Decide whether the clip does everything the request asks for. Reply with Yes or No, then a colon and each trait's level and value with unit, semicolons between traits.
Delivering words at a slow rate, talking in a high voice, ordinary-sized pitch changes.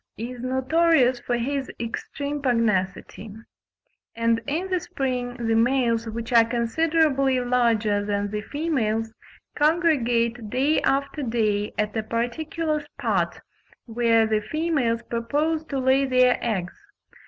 Yes: slow, 125 wpm; high, 245 Hz; average, 3.7 semitones